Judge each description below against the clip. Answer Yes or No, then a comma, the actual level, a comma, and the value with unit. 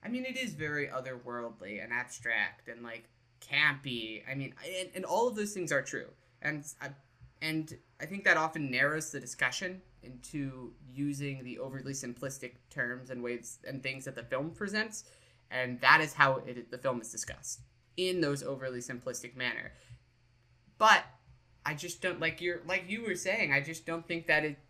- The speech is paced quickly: No, average, 180 wpm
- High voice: No, low, 135 Hz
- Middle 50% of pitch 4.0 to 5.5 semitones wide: Yes, average, 4.6 semitones